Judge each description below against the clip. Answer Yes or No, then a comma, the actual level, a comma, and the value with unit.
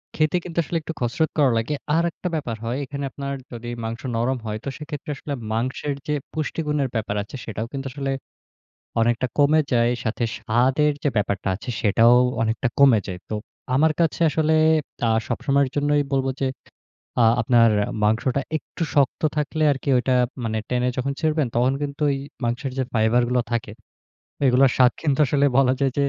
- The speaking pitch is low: Yes, low, 130 Hz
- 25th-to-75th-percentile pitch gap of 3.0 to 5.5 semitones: Yes, average, 3.7 semitones